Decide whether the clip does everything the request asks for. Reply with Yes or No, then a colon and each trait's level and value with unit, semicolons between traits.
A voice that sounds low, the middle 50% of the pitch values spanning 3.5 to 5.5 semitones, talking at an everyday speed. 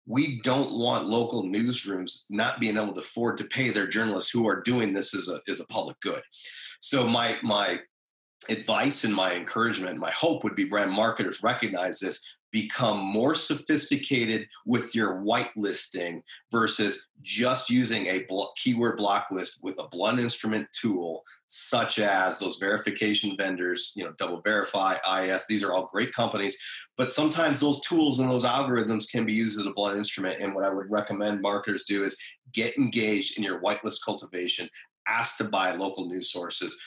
Yes: low, 110 Hz; average, 4.1 semitones; average, 175 wpm